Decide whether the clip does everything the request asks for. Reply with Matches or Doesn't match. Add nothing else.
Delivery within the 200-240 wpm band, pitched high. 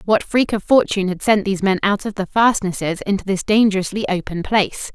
Matches